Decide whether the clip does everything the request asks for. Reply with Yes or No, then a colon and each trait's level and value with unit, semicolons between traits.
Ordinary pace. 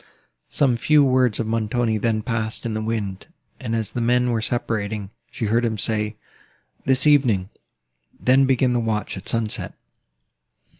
Yes: average, 155 wpm